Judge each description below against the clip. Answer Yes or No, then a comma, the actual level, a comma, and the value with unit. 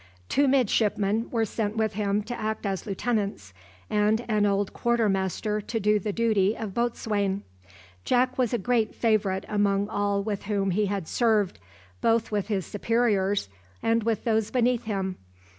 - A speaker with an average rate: Yes, average, 160 wpm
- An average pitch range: No, narrow, 2.3 semitones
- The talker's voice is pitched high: Yes, high, 210 Hz